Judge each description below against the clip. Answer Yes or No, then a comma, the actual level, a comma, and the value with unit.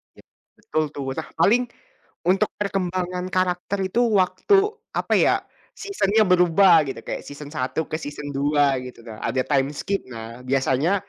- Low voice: No, medium, 165 Hz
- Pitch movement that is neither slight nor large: No, wide, 5.7 semitones